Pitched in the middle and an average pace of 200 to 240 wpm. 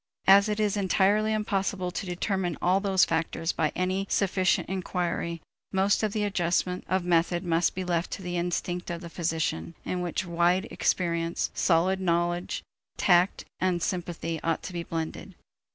No: medium, 180 Hz; average, 160 wpm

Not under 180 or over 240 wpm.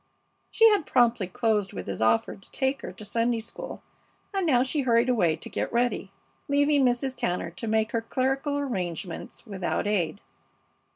No: average, 170 wpm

